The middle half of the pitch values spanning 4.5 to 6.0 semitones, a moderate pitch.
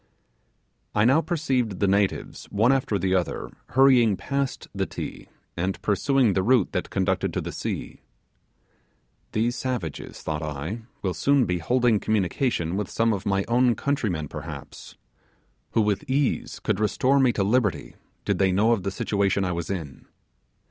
No: average, 5.0 semitones; low, 105 Hz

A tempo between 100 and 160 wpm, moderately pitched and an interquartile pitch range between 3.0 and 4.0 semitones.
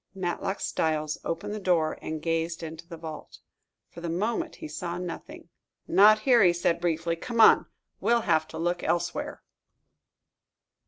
Yes: average, 155 wpm; medium, 175 Hz; average, 3.7 semitones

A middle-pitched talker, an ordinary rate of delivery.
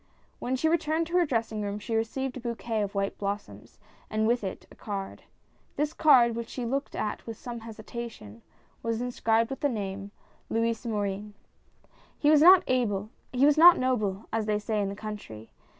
No: high, 225 Hz; average, 170 wpm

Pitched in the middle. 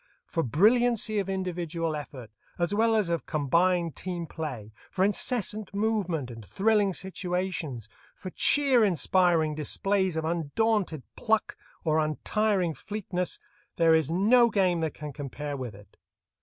Yes: medium, 175 Hz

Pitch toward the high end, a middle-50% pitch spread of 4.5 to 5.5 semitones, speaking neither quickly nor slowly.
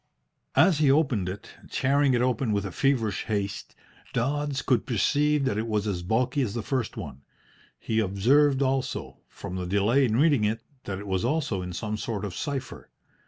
No: low, 115 Hz; average, 5.2 semitones; average, 185 wpm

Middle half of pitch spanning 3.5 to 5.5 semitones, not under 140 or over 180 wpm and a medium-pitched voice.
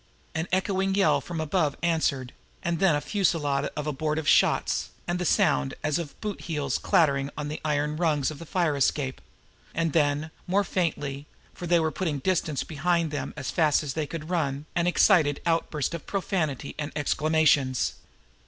No: average, 3.0 semitones; average, 170 wpm; medium, 155 Hz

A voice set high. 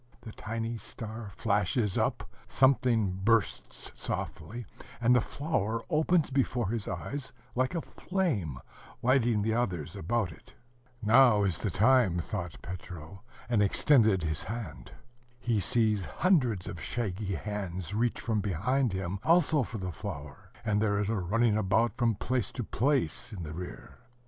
No: low, 110 Hz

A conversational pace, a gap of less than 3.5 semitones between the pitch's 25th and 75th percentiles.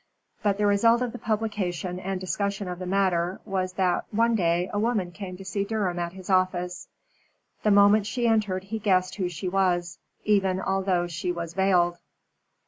Yes: average, 180 wpm; narrow, 2.4 semitones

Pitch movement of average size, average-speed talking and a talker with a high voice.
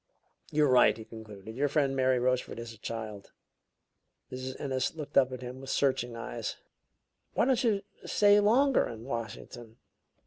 No: average, 3.9 semitones; average, 160 wpm; low, 130 Hz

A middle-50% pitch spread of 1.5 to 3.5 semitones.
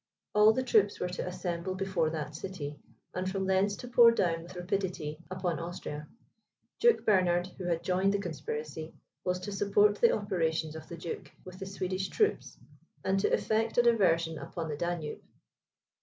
Yes: average, 3.1 semitones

